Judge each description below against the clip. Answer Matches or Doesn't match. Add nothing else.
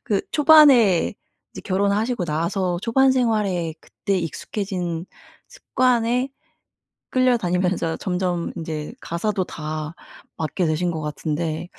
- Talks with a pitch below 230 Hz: Matches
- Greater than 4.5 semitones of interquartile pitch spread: Matches